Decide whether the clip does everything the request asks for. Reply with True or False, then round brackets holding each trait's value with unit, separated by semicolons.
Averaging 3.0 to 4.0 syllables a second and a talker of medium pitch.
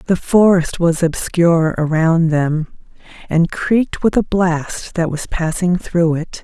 True (3.9 syllables/s; 170 Hz)